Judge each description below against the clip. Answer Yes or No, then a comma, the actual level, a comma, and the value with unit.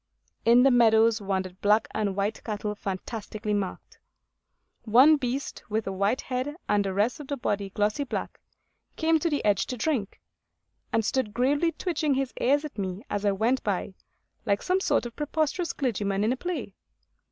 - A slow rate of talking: No, average, 175 wpm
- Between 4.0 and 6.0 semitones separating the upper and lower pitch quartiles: Yes, average, 5.2 semitones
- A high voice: Yes, high, 225 Hz